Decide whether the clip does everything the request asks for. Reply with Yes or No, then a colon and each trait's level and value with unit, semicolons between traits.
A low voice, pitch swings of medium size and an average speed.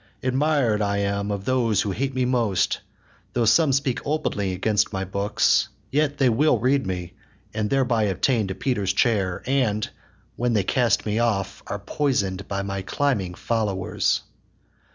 Yes: low, 110 Hz; average, 4.7 semitones; average, 155 wpm